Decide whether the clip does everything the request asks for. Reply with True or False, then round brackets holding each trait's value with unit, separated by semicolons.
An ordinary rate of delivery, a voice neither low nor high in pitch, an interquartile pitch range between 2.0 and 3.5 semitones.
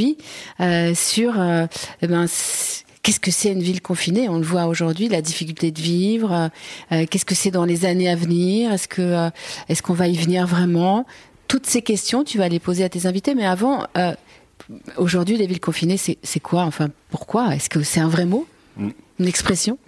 True (200 wpm; 180 Hz; 3.1 semitones)